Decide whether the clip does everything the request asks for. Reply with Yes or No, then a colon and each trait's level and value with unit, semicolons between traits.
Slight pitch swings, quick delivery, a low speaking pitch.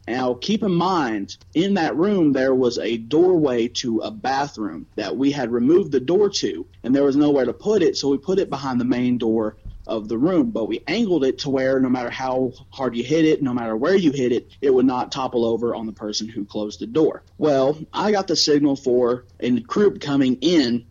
No: average, 4.7 semitones; fast, 230 wpm; low, 130 Hz